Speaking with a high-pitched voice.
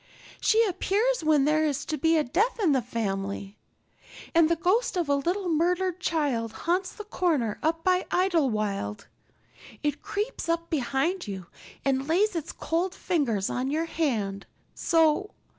Yes: very high, 320 Hz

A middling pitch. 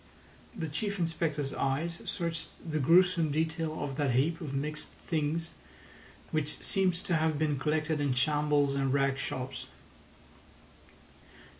Yes: medium, 155 Hz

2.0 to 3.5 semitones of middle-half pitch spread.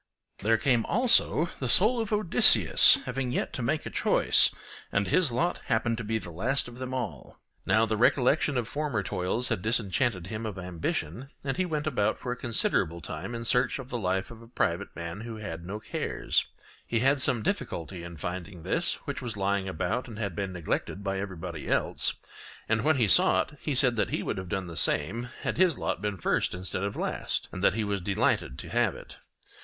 No: average, 5.3 semitones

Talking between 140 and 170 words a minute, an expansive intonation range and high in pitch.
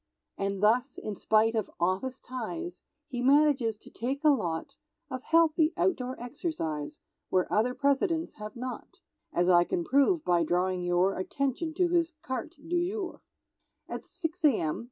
Yes: average, 155 wpm; wide, 8.2 semitones; very high, 255 Hz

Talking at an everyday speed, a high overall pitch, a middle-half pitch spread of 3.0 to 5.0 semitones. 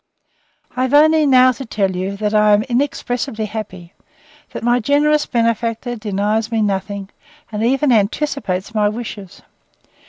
Yes: average, 145 wpm; high, 225 Hz; average, 3.7 semitones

